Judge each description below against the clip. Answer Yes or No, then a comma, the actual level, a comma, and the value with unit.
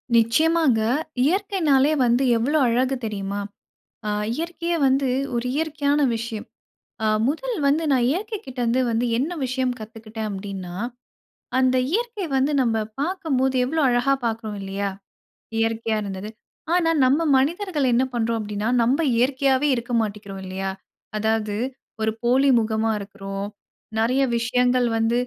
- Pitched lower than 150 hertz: No, high, 245 Hz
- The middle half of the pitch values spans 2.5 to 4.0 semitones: No, average, 4.6 semitones